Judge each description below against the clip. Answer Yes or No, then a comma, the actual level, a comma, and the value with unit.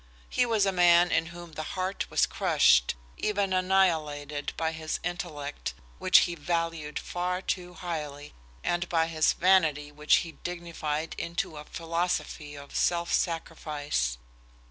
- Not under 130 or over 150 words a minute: Yes, average, 140 wpm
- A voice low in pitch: No, medium, 165 Hz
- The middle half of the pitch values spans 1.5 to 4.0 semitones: Yes, average, 2.8 semitones